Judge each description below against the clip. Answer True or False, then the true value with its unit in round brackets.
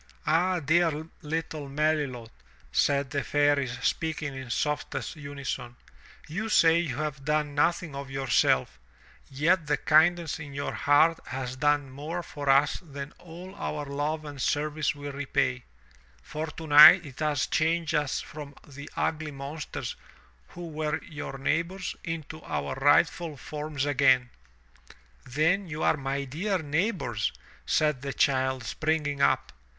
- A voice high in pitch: False (150 Hz)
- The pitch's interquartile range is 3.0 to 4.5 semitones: False (2.4 semitones)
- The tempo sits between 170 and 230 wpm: False (135 wpm)